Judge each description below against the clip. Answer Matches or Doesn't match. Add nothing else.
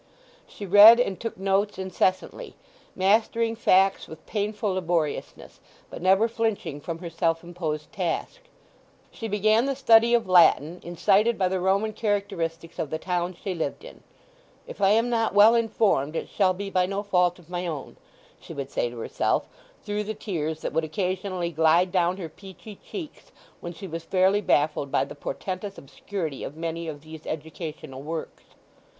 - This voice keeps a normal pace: Matches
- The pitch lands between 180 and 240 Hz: Matches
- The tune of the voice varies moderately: Matches